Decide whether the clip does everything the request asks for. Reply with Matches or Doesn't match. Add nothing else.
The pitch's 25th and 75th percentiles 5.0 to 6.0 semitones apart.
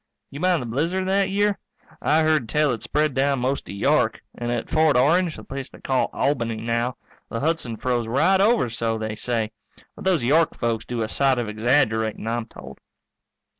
Matches